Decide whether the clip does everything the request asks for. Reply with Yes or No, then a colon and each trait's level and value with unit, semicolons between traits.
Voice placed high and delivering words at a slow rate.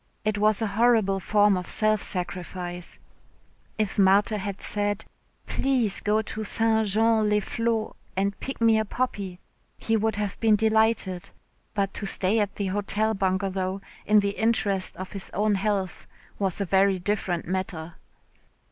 No: high, 205 Hz; average, 155 wpm